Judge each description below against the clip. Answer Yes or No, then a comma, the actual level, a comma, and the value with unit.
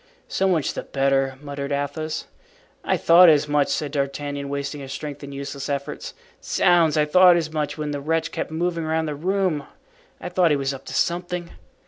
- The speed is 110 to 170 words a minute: No, average, 190 wpm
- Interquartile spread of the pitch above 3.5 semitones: No, average, 2.9 semitones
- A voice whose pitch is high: No, medium, 150 Hz